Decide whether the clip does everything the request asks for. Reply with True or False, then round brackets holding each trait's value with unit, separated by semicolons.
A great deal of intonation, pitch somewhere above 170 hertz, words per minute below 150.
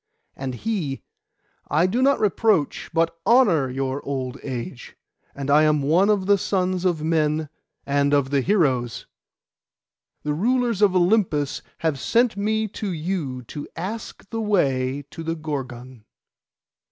False (6.4 semitones; 160 Hz; 140 wpm)